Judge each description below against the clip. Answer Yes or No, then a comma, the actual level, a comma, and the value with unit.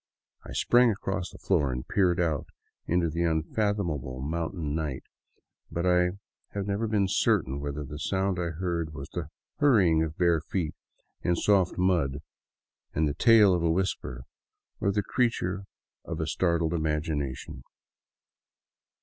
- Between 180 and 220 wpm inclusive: No, average, 145 wpm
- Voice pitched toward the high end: No, very low, 85 Hz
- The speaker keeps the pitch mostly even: No, average, 3.8 semitones